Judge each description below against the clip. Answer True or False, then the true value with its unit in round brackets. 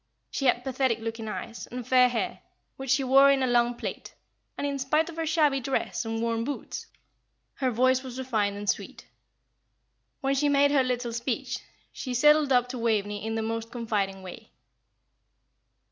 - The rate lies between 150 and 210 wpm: True (175 wpm)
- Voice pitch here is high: True (250 Hz)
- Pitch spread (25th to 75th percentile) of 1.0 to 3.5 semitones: True (3.1 semitones)